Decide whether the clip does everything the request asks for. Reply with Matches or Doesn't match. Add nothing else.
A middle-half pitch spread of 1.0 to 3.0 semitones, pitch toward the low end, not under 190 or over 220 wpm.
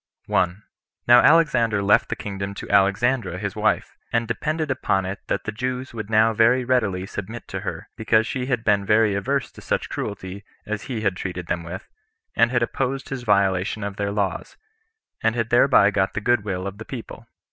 Doesn't match